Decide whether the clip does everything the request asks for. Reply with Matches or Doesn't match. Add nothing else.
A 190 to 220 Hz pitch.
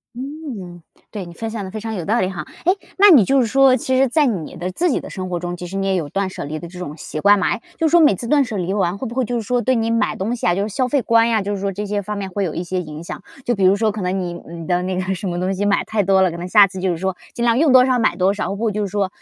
Matches